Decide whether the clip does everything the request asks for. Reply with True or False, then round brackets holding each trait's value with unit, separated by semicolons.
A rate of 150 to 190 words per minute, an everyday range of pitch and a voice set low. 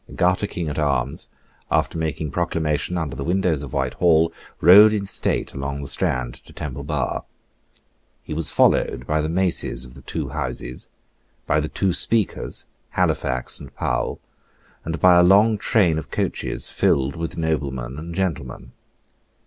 True (155 wpm; 4.4 semitones; 80 Hz)